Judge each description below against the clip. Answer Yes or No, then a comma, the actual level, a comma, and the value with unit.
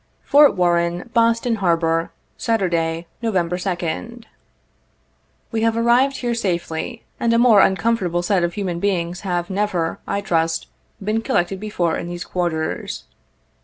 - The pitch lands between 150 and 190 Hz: Yes, medium, 185 Hz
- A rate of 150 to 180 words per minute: No, average, 140 wpm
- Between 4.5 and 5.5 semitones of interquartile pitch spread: Yes, average, 4.8 semitones